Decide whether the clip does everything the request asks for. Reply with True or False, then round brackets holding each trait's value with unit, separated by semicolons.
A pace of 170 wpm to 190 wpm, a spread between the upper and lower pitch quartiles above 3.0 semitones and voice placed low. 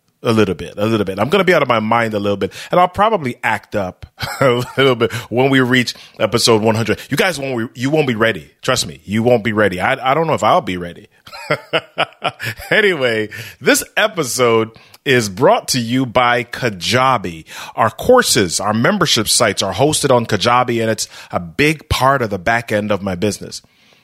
False (200 wpm; 3.6 semitones; 115 Hz)